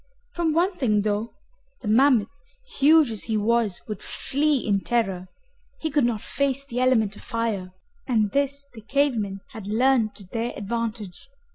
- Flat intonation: No, average, 4.8 semitones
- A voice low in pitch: No, high, 230 Hz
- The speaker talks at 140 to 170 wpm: Yes, average, 165 wpm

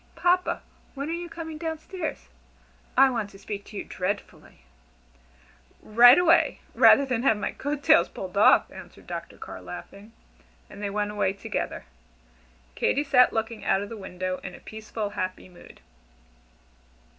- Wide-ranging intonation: Yes, wide, 6.4 semitones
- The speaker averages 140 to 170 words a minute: Yes, average, 155 wpm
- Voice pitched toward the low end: No, high, 225 Hz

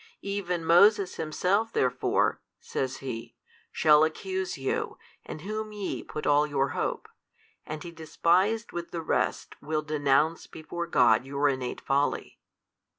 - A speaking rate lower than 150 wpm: Yes, slow, 135 wpm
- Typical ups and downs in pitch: Yes, average, 4.7 semitones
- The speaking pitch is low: No, medium, 155 Hz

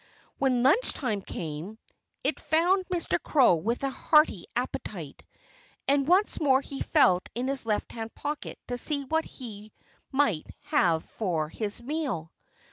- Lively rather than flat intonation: Yes, wide, 6.2 semitones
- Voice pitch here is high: Yes, very high, 260 Hz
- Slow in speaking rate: No, average, 145 wpm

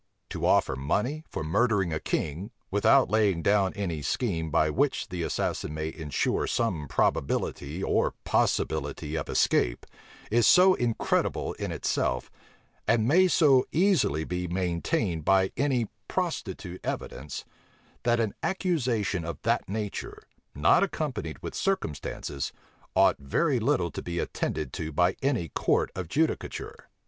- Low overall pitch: Yes, very low, 95 Hz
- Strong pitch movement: Yes, wide, 7.6 semitones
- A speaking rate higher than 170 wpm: No, slow, 135 wpm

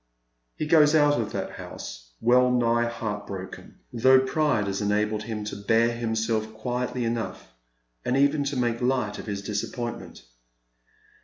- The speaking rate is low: No, average, 150 wpm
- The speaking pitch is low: Yes, low, 115 Hz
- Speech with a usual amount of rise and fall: Yes, average, 3.2 semitones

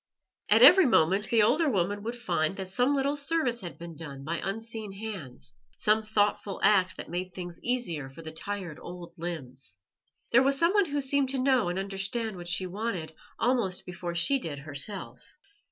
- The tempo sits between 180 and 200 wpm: Yes, average, 185 wpm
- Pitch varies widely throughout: Yes, wide, 5.9 semitones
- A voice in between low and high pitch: No, high, 195 Hz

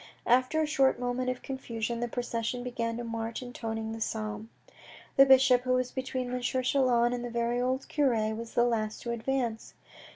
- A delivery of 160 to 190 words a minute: Yes, average, 185 wpm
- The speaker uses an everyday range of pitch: No, narrow, 1.8 semitones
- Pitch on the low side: No, high, 245 Hz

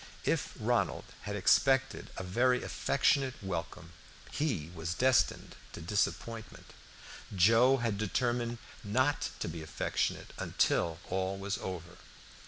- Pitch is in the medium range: No, low, 105 Hz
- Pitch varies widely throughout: Yes, wide, 5.7 semitones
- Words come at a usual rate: No, slow, 115 wpm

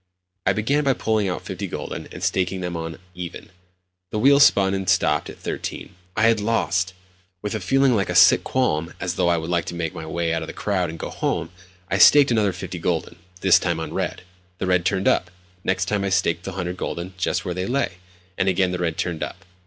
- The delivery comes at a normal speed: No, fast, 225 wpm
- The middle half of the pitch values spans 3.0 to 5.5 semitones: No, narrow, 2.6 semitones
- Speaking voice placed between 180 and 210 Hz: No, very low, 90 Hz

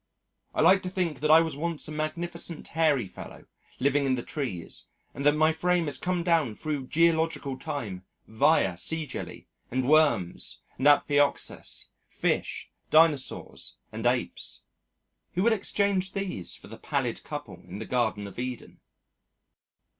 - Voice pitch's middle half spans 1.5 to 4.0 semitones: No, average, 4.6 semitones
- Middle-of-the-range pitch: Yes, medium, 150 Hz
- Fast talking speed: No, average, 150 wpm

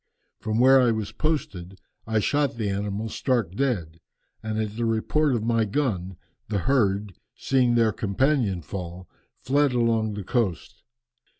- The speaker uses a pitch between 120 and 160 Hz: No, low, 110 Hz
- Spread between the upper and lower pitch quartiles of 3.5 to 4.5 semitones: Yes, average, 4.1 semitones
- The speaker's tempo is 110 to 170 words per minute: Yes, average, 145 wpm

